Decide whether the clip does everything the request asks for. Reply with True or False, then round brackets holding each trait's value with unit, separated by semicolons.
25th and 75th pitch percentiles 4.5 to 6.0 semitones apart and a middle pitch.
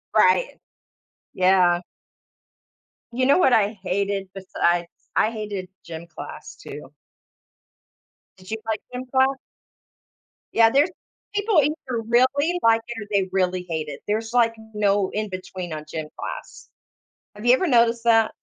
False (4.9 semitones; 215 Hz)